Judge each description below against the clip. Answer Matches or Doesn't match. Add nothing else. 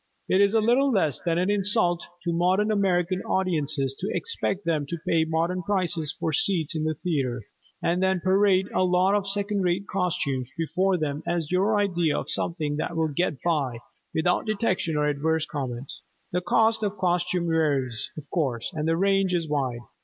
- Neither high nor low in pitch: Matches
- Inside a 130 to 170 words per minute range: Doesn't match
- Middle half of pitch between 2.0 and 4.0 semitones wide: Matches